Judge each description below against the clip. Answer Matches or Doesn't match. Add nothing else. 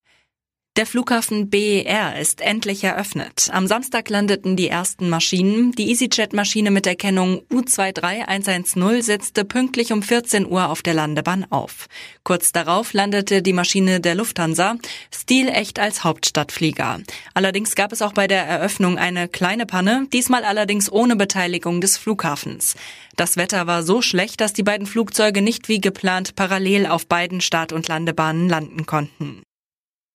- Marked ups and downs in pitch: Doesn't match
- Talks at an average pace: Matches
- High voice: Matches